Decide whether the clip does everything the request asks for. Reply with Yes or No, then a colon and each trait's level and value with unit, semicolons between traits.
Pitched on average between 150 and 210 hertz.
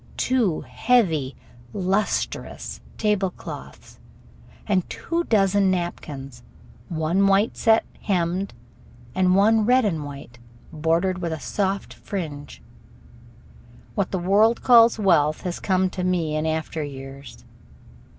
Yes: medium, 185 Hz